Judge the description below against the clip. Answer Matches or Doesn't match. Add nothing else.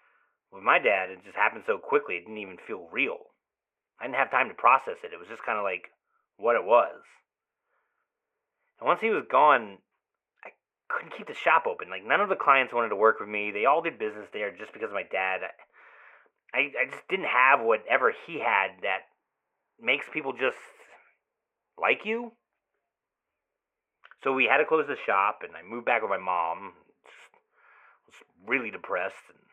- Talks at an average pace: Matches